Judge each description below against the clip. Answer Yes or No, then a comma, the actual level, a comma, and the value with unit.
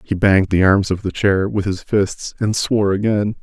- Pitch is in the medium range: No, low, 100 Hz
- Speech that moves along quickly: Yes, fast, 230 wpm